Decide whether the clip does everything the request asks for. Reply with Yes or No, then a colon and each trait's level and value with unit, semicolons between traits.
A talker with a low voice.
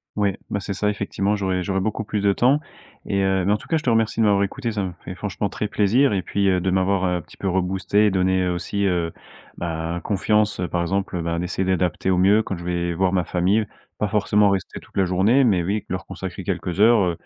Yes: very low, 95 Hz